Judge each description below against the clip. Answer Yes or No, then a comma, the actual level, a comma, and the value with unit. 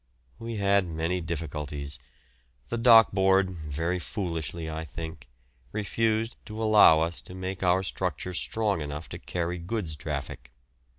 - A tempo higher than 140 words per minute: No, slow, 135 wpm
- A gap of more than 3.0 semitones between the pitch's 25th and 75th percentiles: Yes, average, 4.0 semitones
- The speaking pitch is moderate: No, very low, 90 Hz